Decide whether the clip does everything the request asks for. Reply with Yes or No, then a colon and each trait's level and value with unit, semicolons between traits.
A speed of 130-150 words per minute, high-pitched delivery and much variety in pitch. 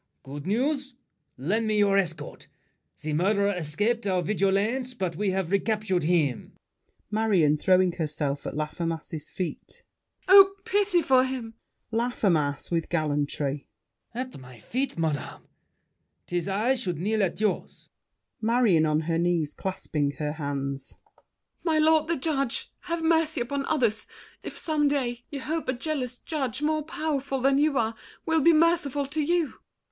Yes: average, 140 wpm; high, 215 Hz; wide, 8.9 semitones